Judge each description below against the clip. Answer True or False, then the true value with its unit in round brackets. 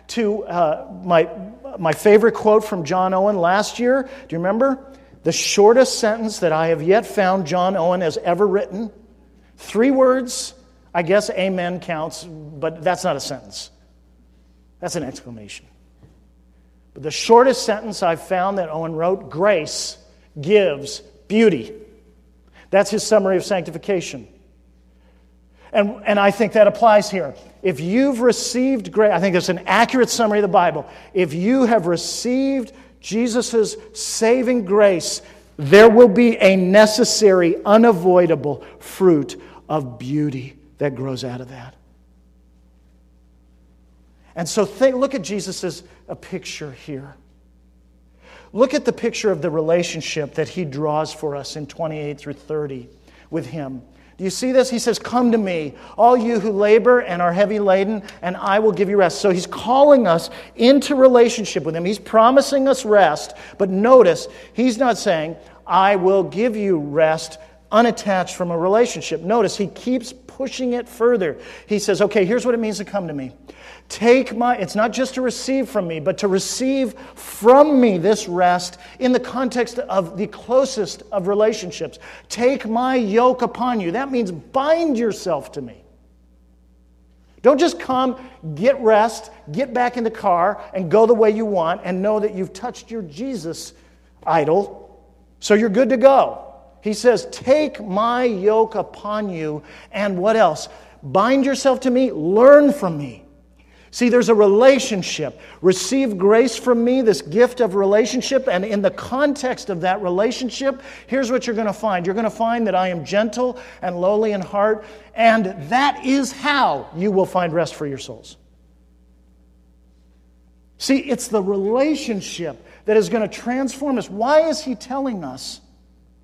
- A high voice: True (205 Hz)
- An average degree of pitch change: False (6.5 semitones)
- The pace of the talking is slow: False (155 wpm)